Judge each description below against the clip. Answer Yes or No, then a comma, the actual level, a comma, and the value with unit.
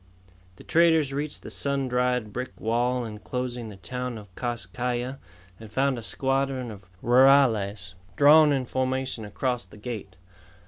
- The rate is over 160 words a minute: No, average, 150 wpm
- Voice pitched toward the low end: Yes, low, 125 Hz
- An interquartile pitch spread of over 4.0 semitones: No, average, 3.4 semitones